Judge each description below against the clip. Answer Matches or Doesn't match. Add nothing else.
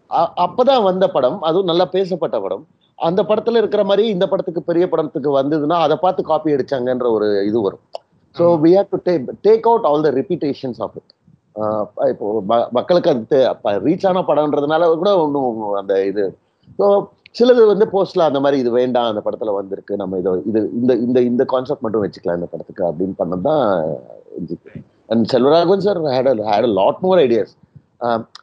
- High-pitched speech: Doesn't match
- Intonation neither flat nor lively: Doesn't match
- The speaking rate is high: Matches